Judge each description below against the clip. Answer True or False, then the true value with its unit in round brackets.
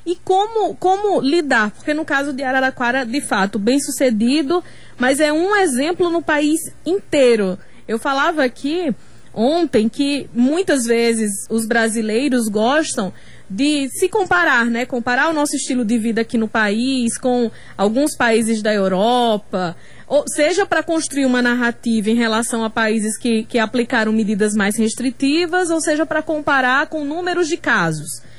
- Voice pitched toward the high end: True (255 Hz)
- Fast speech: False (150 wpm)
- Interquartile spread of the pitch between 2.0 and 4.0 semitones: False (5.3 semitones)